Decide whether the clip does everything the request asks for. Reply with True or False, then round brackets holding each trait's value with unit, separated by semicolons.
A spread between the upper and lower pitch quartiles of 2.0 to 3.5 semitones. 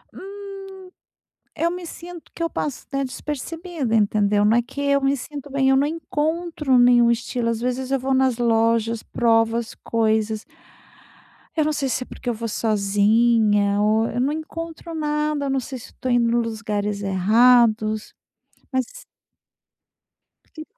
False (4.8 semitones)